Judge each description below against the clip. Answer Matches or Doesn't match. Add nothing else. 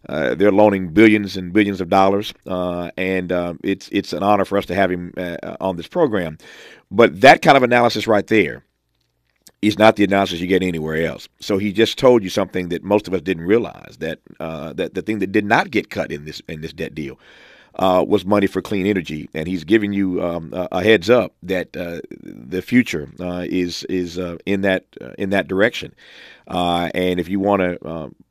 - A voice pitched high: Doesn't match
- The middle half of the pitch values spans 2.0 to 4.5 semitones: Matches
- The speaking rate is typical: Doesn't match